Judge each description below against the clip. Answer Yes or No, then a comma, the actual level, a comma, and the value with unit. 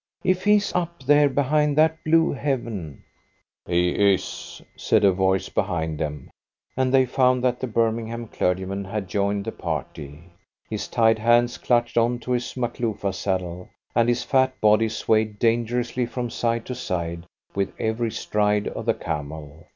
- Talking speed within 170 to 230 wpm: No, average, 160 wpm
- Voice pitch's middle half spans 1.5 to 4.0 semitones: No, average, 4.8 semitones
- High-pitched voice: No, low, 115 Hz